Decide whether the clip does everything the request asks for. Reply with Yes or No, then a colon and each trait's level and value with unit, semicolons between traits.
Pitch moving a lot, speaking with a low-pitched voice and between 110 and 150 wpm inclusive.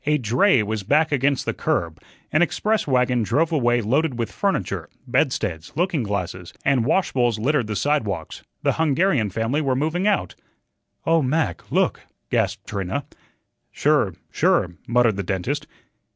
Yes: wide, 6.3 semitones; low, 125 Hz; average, 145 wpm